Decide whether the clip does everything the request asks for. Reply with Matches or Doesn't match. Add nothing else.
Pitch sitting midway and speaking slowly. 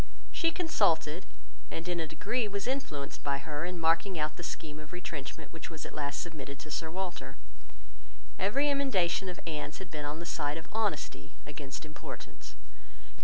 Doesn't match